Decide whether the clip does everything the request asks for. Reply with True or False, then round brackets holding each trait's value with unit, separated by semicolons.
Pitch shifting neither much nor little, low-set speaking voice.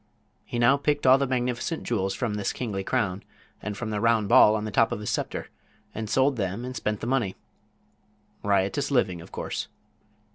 True (4.0 semitones; 110 Hz)